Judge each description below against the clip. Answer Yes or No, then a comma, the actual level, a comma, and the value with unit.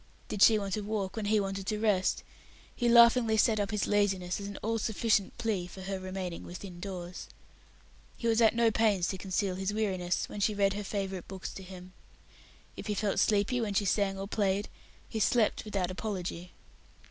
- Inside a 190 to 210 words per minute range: Yes, average, 195 wpm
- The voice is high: Yes, high, 200 Hz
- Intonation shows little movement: Yes, narrow, 2.3 semitones